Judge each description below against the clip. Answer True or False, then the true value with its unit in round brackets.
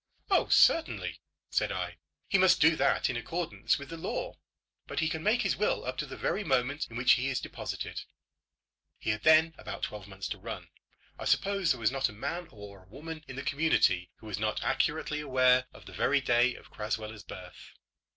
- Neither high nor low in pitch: False (130 Hz)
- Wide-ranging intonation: True (6.8 semitones)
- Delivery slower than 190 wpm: False (200 wpm)